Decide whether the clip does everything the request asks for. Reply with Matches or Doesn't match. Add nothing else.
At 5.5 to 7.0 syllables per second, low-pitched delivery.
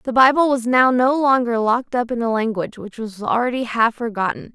Doesn't match